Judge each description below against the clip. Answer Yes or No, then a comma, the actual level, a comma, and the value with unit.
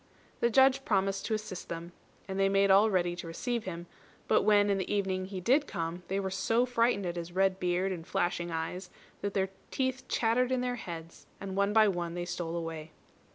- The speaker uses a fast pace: Yes, fast, 210 wpm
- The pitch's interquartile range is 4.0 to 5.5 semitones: No, average, 3.6 semitones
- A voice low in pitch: No, high, 190 Hz